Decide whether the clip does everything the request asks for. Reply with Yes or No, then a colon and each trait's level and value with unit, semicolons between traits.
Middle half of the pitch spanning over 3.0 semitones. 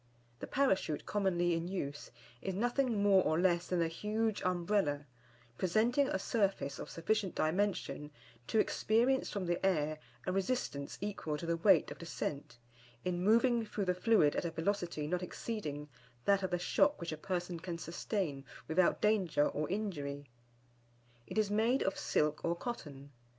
Yes: average, 4.5 semitones